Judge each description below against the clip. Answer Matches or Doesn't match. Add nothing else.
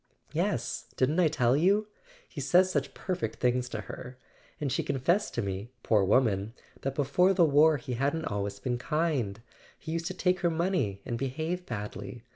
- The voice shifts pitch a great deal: Matches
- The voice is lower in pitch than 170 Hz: Matches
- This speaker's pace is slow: Doesn't match